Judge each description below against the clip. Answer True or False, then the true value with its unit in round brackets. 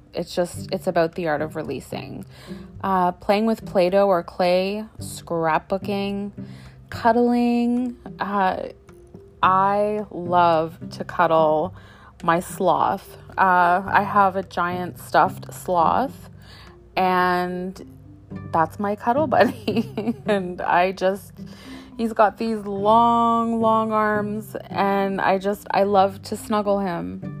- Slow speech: True (115 wpm)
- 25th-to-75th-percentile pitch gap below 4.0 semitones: True (3.3 semitones)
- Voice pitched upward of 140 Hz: True (190 Hz)